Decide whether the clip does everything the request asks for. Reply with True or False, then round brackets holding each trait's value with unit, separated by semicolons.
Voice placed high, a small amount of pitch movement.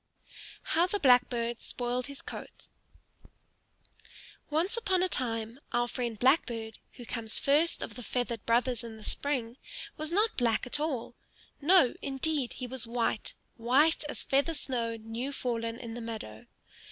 False (245 Hz; 3.7 semitones)